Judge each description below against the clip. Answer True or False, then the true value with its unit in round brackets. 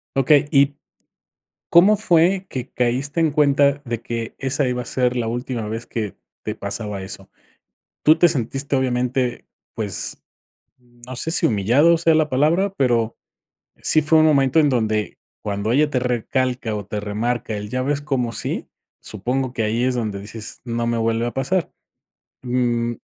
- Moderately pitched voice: False (125 Hz)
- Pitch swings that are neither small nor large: True (3.7 semitones)